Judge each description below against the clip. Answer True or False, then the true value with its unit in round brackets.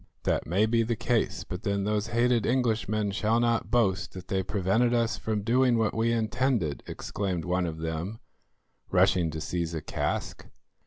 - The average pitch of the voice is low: True (105 Hz)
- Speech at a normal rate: True (170 wpm)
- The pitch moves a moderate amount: True (4.2 semitones)